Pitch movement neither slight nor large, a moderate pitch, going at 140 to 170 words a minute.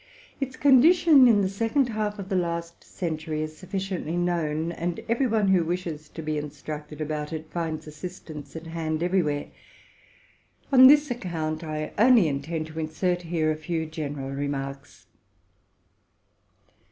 Yes: average, 3.9 semitones; medium, 165 Hz; average, 150 wpm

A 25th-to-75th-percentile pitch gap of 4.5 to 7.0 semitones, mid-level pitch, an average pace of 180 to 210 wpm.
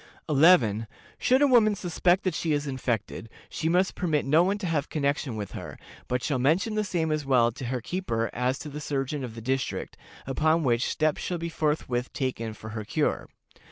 Yes: average, 5.2 semitones; medium, 145 Hz; average, 200 wpm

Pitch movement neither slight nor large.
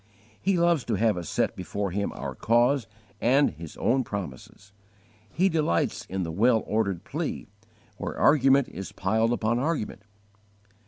No: wide, 5.9 semitones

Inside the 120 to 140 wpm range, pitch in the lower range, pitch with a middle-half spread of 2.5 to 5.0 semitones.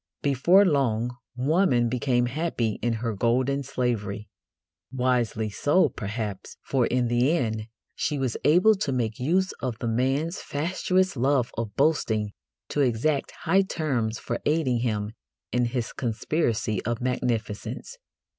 Yes: slow, 135 wpm; low, 125 Hz; average, 4.3 semitones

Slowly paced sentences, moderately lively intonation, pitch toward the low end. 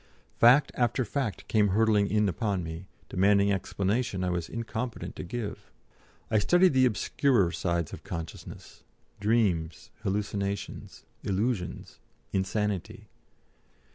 Yes: slow, 110 wpm; average, 3.6 semitones; low, 100 Hz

